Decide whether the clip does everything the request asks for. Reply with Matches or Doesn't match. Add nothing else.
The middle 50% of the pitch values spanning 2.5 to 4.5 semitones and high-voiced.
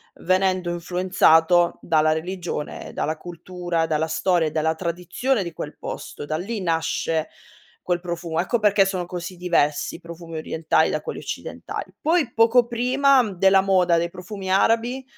Doesn't match